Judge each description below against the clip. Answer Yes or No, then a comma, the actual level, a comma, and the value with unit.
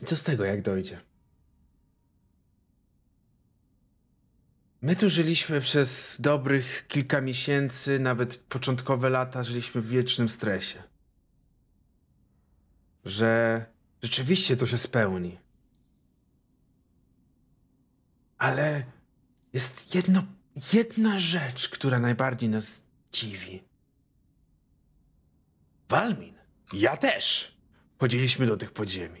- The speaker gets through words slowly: Yes, slow, 80 wpm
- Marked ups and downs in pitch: Yes, wide, 6.7 semitones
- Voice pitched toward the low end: Yes, low, 125 Hz